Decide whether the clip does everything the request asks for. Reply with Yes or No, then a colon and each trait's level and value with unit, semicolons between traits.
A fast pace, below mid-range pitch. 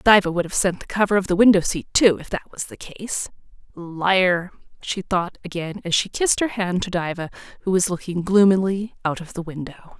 No: fast, 210 wpm; medium, 185 Hz